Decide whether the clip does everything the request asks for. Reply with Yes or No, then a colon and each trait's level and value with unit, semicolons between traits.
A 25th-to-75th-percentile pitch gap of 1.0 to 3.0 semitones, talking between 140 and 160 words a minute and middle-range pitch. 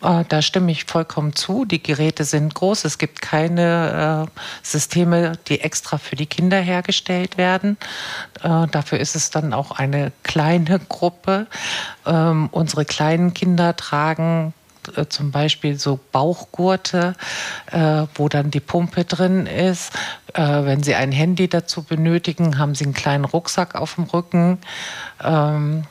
Yes: average, 2.7 semitones; average, 145 wpm; medium, 160 Hz